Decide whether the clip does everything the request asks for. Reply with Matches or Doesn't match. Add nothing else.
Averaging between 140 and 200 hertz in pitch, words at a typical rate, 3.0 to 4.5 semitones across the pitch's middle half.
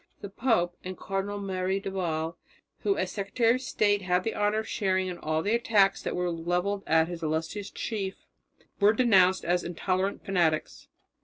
Doesn't match